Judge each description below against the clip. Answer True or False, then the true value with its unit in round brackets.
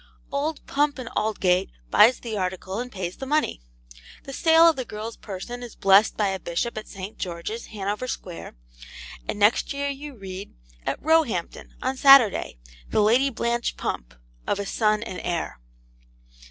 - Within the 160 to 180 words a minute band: True (165 wpm)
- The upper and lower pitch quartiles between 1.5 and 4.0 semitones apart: False (5.5 semitones)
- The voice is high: True (220 Hz)